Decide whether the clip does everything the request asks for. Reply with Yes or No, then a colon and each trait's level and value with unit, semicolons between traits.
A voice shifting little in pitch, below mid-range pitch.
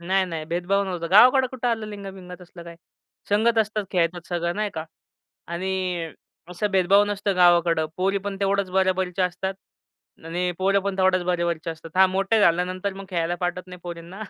No: narrow, 2.3 semitones; medium, 185 Hz